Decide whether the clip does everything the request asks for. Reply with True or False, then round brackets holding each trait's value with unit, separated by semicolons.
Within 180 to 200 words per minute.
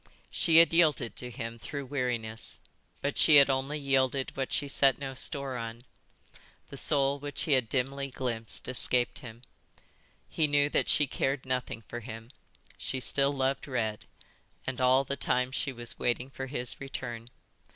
False (165 wpm)